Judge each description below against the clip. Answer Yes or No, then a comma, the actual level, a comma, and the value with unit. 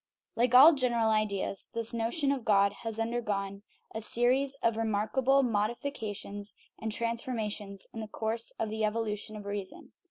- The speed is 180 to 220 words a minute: No, average, 155 wpm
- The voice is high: Yes, high, 225 Hz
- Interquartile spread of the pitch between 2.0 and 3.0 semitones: Yes, narrow, 2.4 semitones